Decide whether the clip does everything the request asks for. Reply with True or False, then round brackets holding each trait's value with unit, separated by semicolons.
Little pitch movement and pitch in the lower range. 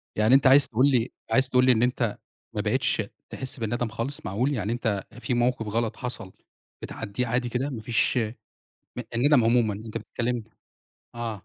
True (2.2 semitones; 120 Hz)